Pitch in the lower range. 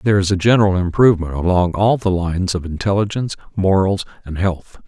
Yes: very low, 95 Hz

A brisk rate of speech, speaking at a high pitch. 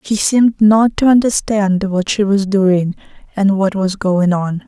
No: average, 180 wpm; high, 200 Hz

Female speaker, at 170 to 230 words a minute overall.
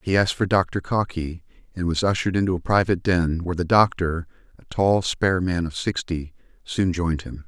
No: male; average, 195 wpm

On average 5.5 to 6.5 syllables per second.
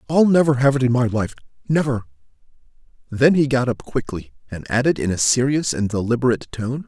Yes: 5.9 syllables/s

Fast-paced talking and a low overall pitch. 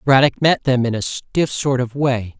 Yes: fast, 250 wpm; low, 130 Hz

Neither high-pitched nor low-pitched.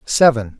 No: low, 125 Hz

